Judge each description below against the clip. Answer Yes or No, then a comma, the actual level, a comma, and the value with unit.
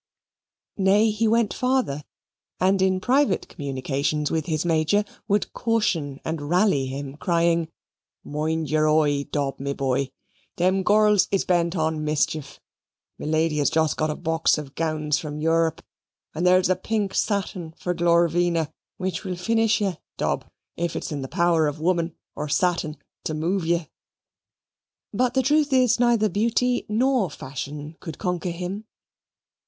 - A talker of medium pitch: Yes, medium, 170 Hz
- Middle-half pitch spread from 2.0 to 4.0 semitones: No, average, 4.5 semitones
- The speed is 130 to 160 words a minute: Yes, average, 150 wpm